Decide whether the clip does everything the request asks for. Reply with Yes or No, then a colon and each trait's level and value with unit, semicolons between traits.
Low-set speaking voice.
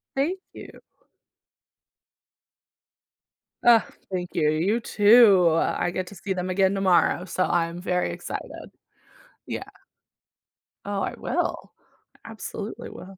No: high, 190 Hz